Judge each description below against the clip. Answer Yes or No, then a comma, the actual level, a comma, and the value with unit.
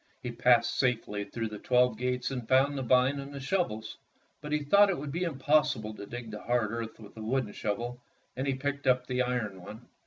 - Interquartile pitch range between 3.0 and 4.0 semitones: Yes, average, 3.5 semitones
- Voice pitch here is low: Yes, low, 125 Hz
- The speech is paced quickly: Yes, fast, 220 wpm